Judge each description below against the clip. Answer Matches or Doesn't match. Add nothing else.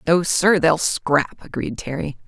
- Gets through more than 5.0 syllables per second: Doesn't match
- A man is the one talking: Doesn't match